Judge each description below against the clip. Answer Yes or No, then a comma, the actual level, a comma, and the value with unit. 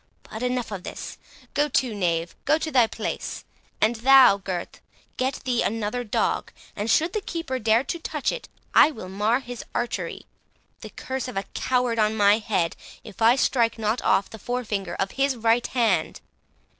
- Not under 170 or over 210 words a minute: Yes, average, 175 wpm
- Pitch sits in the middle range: No, high, 235 Hz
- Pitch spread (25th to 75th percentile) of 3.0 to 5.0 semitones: Yes, average, 3.7 semitones